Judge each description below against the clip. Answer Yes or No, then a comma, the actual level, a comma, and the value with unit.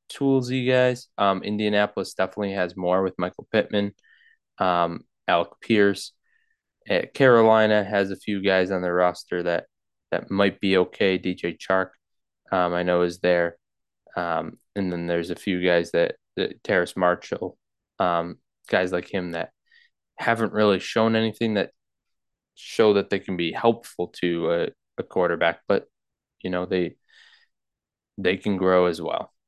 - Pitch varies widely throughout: No, average, 3.1 semitones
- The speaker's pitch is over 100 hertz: No, very low, 95 Hz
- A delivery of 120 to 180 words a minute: Yes, average, 155 wpm